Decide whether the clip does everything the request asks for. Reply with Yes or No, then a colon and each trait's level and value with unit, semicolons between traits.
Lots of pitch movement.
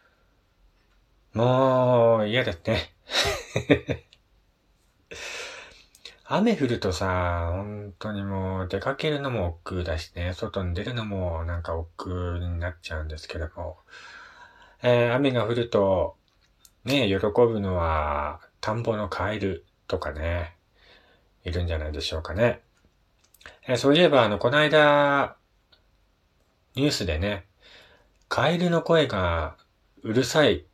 Yes: wide, 5.9 semitones